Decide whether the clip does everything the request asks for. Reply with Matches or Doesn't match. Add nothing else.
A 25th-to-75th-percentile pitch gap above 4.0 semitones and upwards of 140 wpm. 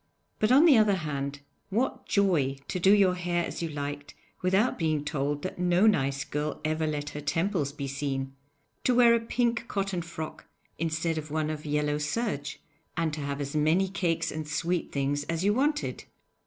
Matches